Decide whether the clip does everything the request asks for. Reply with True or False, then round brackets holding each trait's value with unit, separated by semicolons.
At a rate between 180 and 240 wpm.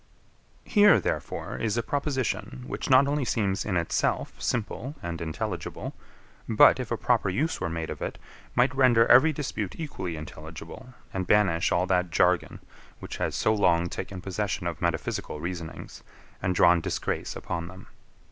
False (160 wpm)